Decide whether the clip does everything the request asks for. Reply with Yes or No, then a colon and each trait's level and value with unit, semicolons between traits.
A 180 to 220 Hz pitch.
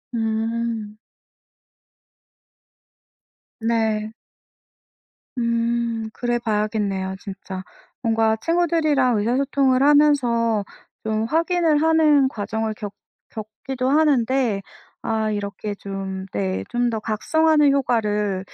No: high, 230 Hz